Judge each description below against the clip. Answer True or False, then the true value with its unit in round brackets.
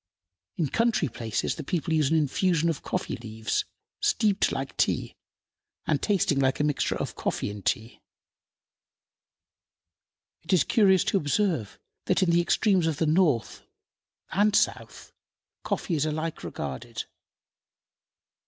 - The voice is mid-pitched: True (160 Hz)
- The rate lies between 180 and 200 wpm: False (135 wpm)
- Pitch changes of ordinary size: False (5.8 semitones)